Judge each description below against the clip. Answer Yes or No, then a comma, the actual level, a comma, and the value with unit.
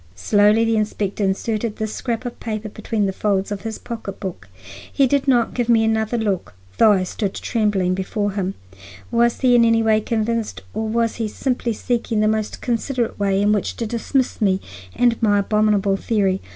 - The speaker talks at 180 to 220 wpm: Yes, average, 190 wpm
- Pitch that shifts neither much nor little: No, narrow, 2.3 semitones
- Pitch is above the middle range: Yes, high, 215 Hz